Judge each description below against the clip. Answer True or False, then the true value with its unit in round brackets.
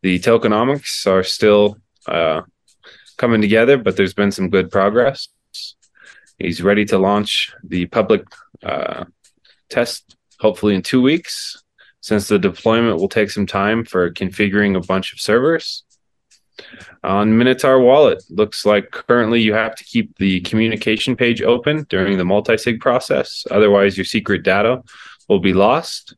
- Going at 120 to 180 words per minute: True (145 wpm)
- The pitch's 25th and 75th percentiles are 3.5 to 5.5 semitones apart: False (3.0 semitones)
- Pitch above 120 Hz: False (105 Hz)